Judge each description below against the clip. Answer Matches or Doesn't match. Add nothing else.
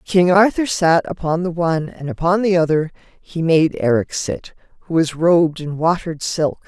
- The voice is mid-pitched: Matches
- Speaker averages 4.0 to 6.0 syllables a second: Matches